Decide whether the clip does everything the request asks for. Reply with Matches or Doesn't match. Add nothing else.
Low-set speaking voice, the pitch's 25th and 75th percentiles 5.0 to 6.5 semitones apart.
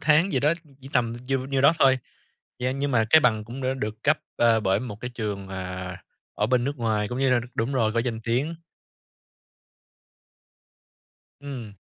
Doesn't match